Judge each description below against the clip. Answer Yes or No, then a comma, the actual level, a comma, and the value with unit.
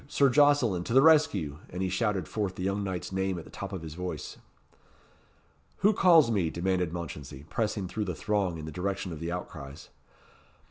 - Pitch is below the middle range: Yes, very low, 95 Hz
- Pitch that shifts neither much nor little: Yes, average, 4.0 semitones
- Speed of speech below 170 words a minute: No, average, 190 wpm